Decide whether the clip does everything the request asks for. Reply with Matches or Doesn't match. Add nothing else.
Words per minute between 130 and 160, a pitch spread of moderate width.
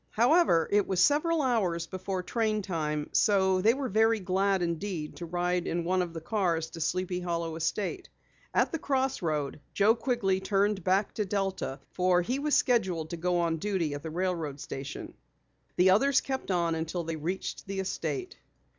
Doesn't match